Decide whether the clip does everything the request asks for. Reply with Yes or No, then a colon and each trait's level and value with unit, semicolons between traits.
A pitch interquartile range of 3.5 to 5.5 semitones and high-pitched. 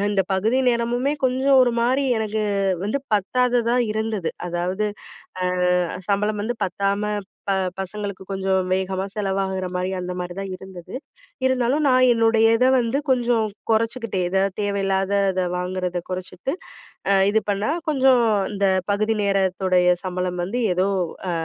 Yes: average, 3.8 semitones; high, 200 Hz